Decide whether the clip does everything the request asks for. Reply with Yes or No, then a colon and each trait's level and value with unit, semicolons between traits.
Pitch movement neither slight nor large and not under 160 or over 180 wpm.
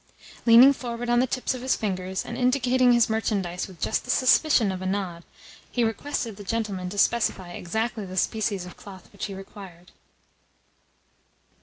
Yes: average, 4.2 semitones; average, 170 wpm